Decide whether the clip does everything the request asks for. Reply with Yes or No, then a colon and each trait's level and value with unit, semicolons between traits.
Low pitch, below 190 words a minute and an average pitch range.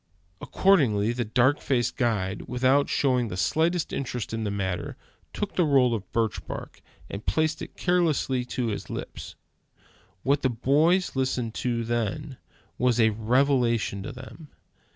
Yes: low, 125 Hz; average, 150 wpm; average, 4.0 semitones